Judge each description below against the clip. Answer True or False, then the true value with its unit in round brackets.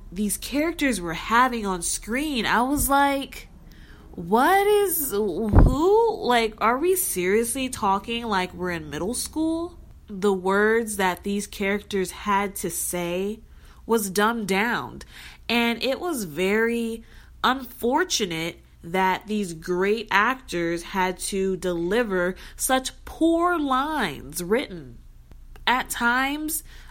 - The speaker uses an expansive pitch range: True (5.7 semitones)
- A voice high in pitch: True (215 Hz)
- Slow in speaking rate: True (115 wpm)